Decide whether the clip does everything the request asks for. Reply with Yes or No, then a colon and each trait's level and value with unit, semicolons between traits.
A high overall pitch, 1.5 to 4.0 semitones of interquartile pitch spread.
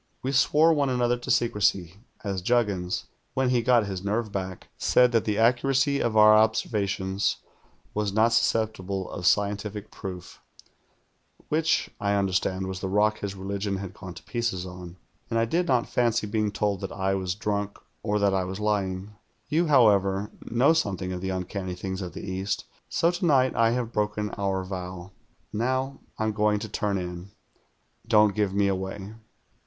No: low, 105 Hz; average, 3.4 semitones